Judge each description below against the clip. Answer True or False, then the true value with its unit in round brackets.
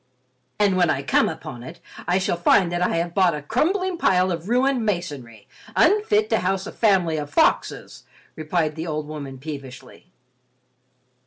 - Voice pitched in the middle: True (175 Hz)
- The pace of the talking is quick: False (165 wpm)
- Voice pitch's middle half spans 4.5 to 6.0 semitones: True (5.1 semitones)